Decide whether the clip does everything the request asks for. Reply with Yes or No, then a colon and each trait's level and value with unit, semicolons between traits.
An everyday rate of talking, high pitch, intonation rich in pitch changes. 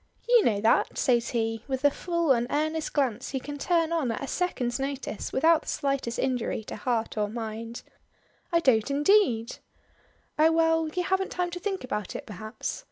Yes: average, 185 wpm; very high, 270 Hz; wide, 5.9 semitones